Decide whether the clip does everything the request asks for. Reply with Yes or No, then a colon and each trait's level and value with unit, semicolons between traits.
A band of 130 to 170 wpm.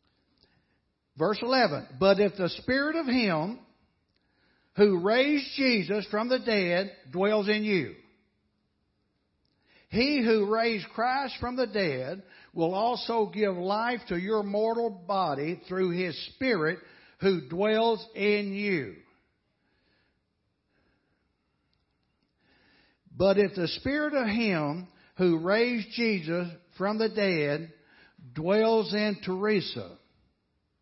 No: slow, 105 wpm